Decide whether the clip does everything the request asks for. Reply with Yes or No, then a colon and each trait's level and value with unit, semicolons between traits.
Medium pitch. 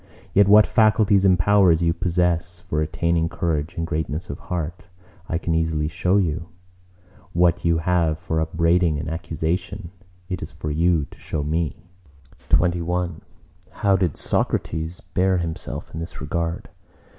No: very low, 85 Hz